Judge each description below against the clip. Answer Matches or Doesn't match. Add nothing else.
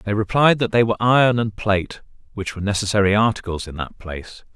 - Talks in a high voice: Doesn't match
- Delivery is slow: Doesn't match